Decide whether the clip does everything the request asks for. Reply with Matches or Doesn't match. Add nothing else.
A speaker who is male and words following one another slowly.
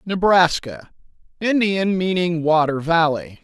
Matches